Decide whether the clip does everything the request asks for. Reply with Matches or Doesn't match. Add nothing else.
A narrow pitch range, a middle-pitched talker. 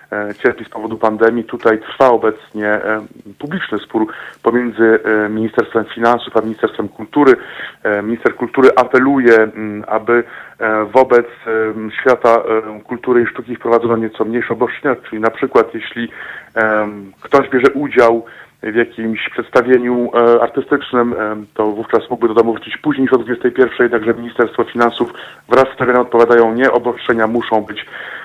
Doesn't match